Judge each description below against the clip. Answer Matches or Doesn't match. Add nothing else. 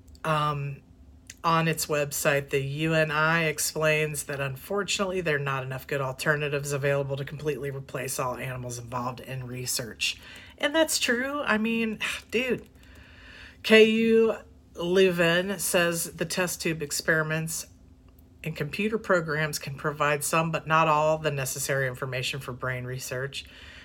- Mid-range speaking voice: Matches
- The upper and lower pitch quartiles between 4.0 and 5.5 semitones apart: Matches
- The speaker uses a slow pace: Matches